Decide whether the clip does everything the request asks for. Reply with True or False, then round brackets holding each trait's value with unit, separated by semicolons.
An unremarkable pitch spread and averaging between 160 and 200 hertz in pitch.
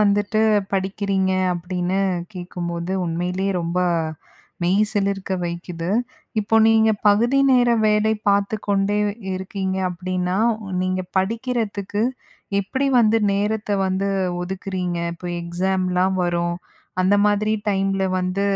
False (2.2 semitones; 190 Hz)